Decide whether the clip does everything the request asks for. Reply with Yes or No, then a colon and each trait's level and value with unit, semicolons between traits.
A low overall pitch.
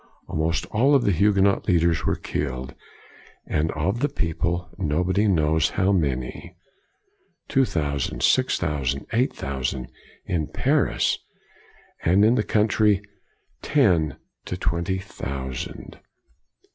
Yes: very low, 85 Hz